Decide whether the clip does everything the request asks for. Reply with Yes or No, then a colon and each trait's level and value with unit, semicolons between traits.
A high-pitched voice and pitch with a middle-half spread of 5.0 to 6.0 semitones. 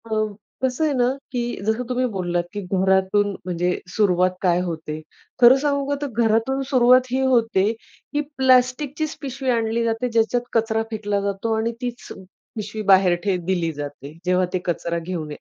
Yes: high, 220 Hz; average, 5.3 semitones